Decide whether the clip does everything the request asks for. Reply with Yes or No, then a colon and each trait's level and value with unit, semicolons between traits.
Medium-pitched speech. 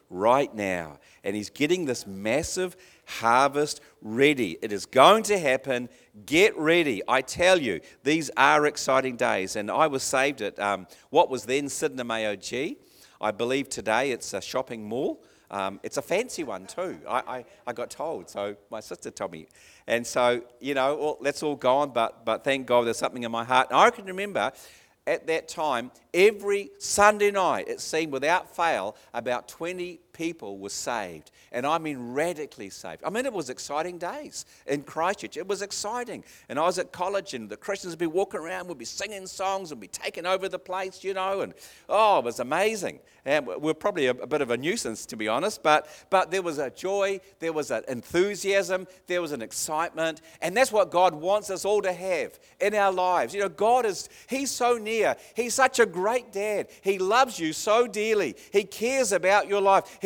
Yes: medium, 175 Hz